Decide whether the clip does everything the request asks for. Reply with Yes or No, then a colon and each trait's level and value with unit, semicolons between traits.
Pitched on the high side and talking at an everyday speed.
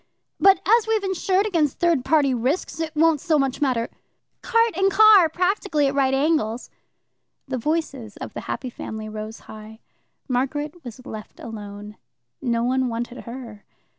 Yes: very high, 275 Hz; average, 175 wpm